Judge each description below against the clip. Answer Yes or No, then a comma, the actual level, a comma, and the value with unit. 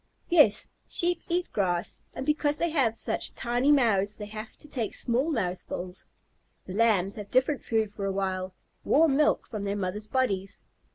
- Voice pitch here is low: No, high, 220 Hz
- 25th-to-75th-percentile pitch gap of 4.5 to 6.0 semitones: Yes, wide, 5.6 semitones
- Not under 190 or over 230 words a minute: No, average, 170 wpm